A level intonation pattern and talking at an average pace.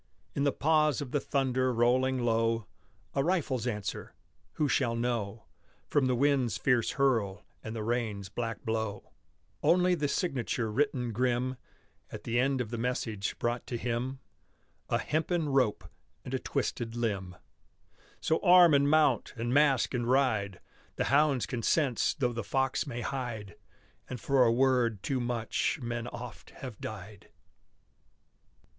No: average, 3.1 semitones; average, 150 wpm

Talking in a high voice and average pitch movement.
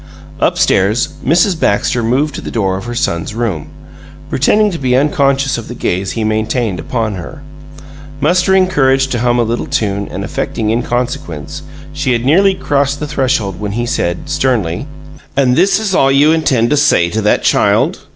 No: low, 125 Hz; average, 5.0 semitones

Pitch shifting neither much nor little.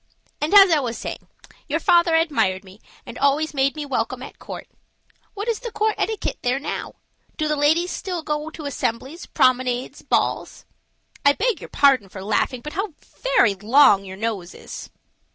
No: wide, 5.9 semitones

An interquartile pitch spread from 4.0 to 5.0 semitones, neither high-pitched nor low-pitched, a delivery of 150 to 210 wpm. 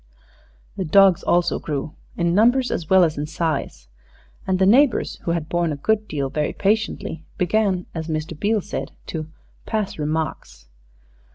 Yes: average, 4.5 semitones; medium, 170 Hz; average, 160 wpm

